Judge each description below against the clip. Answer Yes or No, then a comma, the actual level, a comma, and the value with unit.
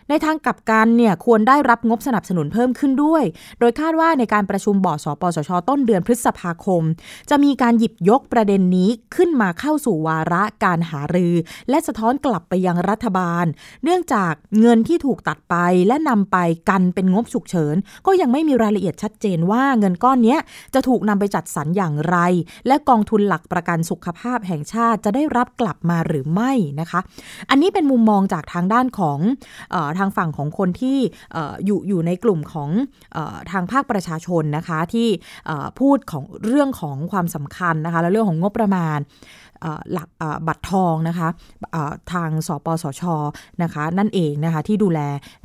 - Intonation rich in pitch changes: Yes, wide, 5.9 semitones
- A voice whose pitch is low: No, high, 195 Hz